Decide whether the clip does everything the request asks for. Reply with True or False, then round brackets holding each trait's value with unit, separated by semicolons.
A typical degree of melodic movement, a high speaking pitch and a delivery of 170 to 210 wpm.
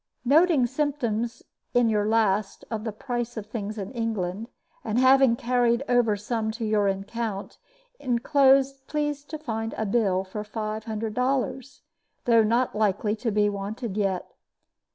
False (3.1 semitones; 225 Hz; 150 wpm)